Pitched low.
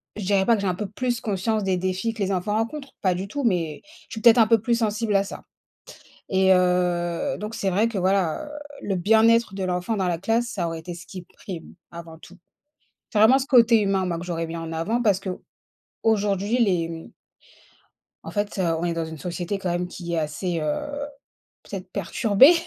No: high, 195 Hz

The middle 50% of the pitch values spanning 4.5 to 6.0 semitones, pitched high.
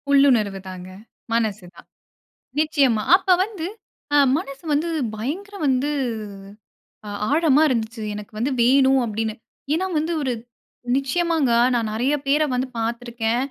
Yes: average, 5.0 semitones; very high, 265 Hz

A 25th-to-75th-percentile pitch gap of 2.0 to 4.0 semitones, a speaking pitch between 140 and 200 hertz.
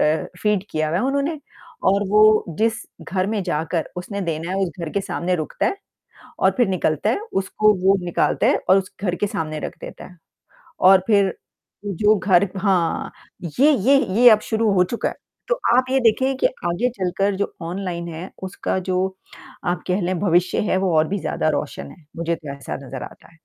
Yes: average, 3.4 semitones; high, 190 Hz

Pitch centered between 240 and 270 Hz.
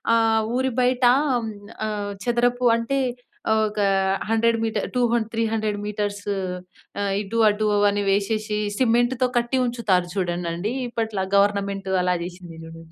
No: high, 215 Hz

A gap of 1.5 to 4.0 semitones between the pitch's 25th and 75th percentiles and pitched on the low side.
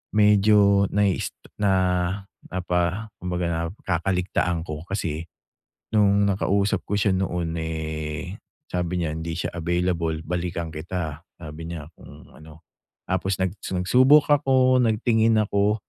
Yes: average, 3.5 semitones; very low, 90 Hz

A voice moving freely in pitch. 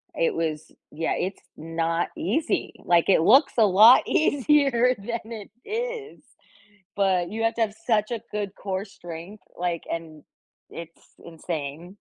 Yes: wide, 5.8 semitones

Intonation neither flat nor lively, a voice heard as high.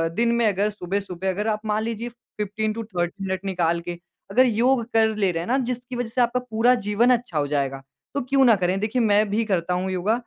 Yes: average, 4.0 semitones; high, 215 Hz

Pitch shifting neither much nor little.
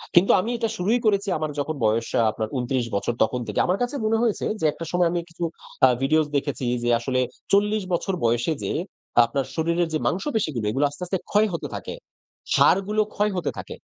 No: wide, 6.9 semitones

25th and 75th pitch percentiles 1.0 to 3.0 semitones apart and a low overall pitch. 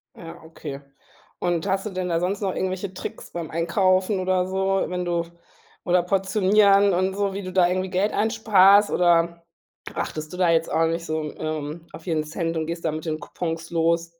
No: narrow, 2.5 semitones; medium, 180 Hz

